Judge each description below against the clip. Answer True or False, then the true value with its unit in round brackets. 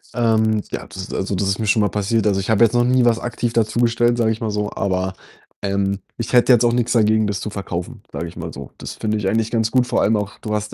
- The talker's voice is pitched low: True (110 Hz)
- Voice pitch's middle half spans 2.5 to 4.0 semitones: True (2.8 semitones)